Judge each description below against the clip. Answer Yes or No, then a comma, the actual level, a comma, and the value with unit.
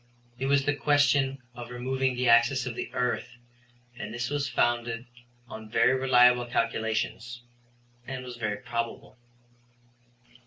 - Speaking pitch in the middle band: No, low, 125 Hz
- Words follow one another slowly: Yes, slow, 130 wpm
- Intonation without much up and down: Yes, narrow, 2.0 semitones